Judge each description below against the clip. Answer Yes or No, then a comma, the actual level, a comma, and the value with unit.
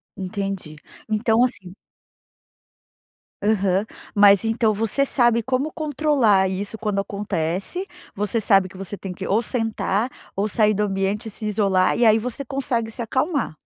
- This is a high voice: Yes, high, 210 Hz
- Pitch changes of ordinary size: Yes, average, 3.3 semitones